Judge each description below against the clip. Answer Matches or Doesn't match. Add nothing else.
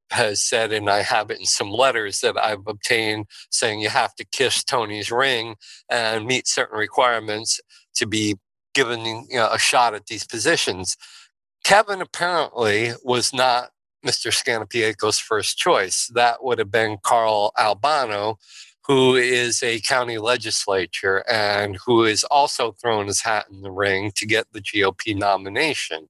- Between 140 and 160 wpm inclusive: Matches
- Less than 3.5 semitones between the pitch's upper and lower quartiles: Matches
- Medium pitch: Doesn't match